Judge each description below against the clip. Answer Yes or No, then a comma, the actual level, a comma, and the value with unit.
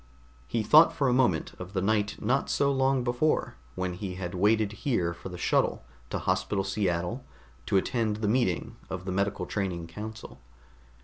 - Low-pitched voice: Yes, low, 105 Hz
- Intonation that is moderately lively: Yes, average, 4.8 semitones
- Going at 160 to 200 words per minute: Yes, average, 175 wpm